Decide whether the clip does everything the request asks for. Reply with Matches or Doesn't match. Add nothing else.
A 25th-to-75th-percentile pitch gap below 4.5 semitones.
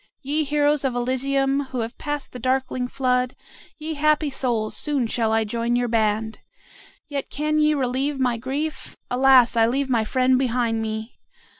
Matches